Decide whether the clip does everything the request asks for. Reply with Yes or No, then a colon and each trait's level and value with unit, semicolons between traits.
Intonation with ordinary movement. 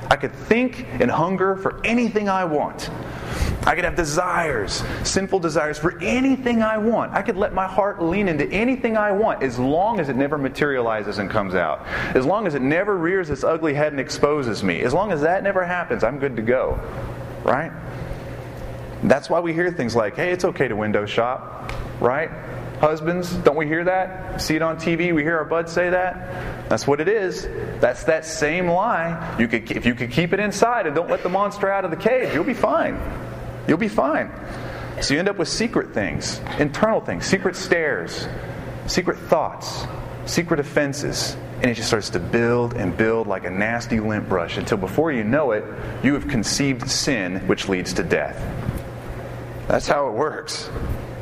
No: wide, 6.3 semitones